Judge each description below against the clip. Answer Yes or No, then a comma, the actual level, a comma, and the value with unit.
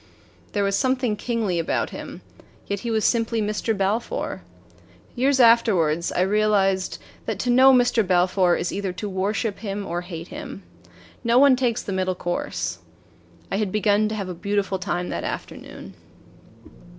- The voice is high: Yes, high, 205 Hz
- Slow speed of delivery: No, average, 160 wpm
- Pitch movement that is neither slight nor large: Yes, average, 3.8 semitones